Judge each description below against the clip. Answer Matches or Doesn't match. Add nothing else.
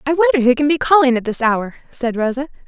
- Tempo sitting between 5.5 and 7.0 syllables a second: Matches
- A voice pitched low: Doesn't match